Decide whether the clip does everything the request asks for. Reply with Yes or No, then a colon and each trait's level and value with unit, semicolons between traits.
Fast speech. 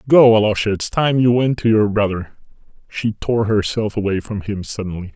No: average, 185 wpm